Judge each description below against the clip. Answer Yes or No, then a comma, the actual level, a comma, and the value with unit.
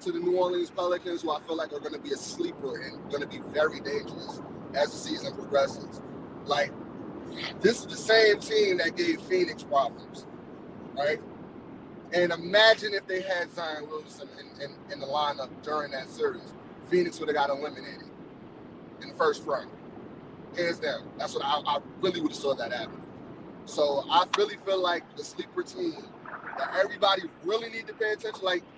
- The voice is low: No, high, 190 Hz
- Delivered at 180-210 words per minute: Yes, average, 185 wpm